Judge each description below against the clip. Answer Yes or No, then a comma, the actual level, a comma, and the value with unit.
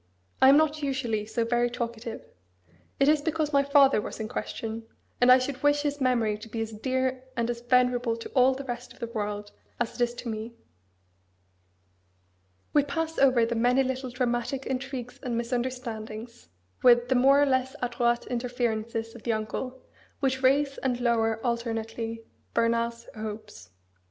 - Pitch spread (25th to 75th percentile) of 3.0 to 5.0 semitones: No, narrow, 2.4 semitones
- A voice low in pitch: No, high, 240 Hz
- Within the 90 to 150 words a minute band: No, average, 170 wpm